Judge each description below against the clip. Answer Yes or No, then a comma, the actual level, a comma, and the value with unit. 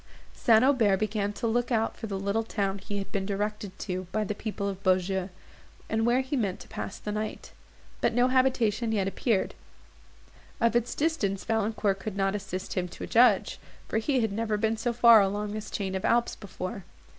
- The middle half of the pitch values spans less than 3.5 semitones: Yes, narrow, 2.6 semitones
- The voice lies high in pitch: Yes, high, 210 Hz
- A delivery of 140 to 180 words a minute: No, average, 195 wpm